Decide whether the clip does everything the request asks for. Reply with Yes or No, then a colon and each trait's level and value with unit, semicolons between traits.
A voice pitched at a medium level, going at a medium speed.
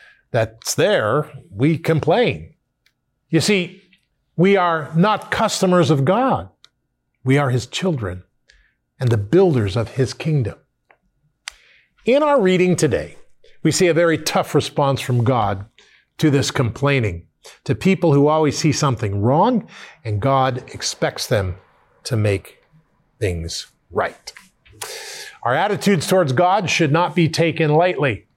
No: medium, 155 Hz; slow, 130 wpm